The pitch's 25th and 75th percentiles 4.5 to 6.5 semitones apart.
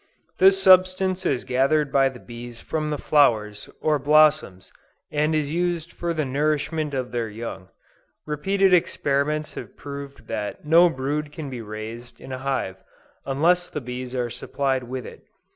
No: average, 3.9 semitones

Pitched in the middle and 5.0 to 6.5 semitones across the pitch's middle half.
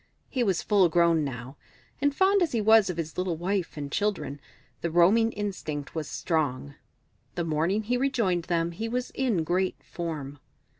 Yes: medium, 175 Hz; wide, 5.6 semitones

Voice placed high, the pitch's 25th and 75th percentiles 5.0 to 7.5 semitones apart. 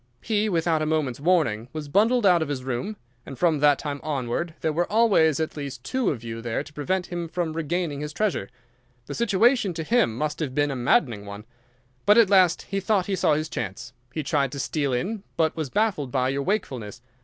No: medium, 155 Hz; wide, 5.6 semitones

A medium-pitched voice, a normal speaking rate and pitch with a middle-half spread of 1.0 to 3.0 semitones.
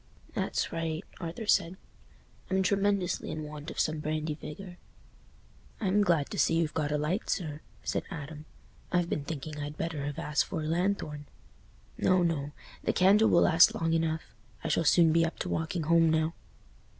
Yes: medium, 165 Hz; average, 175 wpm; average, 2.7 semitones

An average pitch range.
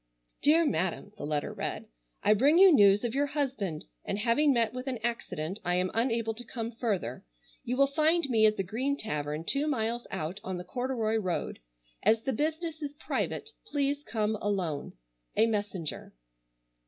No: wide, 5.9 semitones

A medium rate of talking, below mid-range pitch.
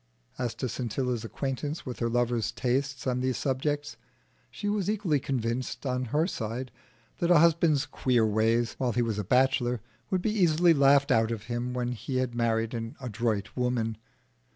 Yes: average, 175 wpm; low, 125 Hz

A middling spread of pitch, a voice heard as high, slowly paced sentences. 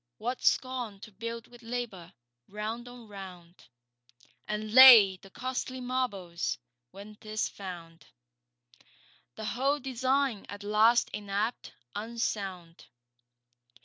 Yes: average, 3.8 semitones; high, 215 Hz; slow, 105 wpm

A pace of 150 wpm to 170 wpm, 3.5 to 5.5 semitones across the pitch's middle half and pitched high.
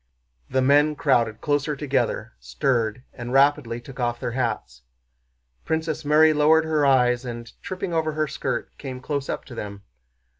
No: average, 155 wpm; average, 3.9 semitones; low, 135 Hz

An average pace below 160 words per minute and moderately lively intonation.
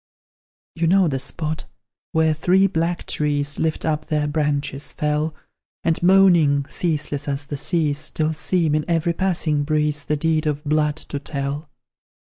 No: average, 150 wpm; narrow, 2.0 semitones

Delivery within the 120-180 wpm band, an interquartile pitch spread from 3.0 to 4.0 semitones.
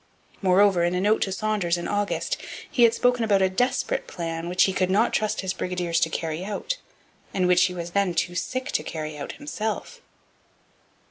No: average, 195 wpm; average, 3.6 semitones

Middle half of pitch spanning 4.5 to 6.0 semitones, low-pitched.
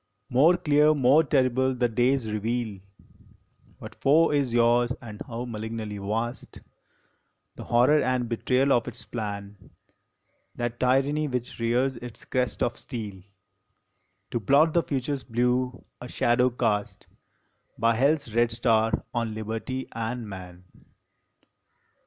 No: average, 2.7 semitones; low, 120 Hz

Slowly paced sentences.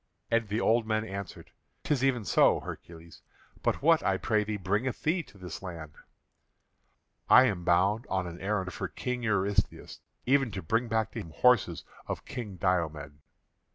No: average, 165 wpm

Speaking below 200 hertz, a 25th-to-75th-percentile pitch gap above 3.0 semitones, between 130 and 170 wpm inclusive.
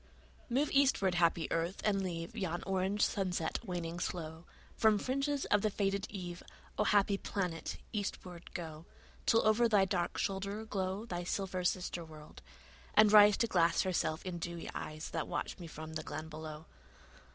Yes: medium, 185 Hz; average, 3.6 semitones; average, 165 wpm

